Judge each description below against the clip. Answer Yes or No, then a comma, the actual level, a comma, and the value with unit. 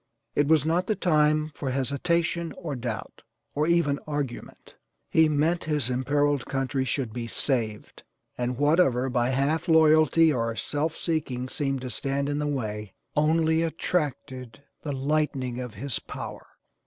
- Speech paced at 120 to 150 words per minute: Yes, average, 145 wpm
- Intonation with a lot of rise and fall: No, average, 3.6 semitones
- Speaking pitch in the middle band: Yes, medium, 145 Hz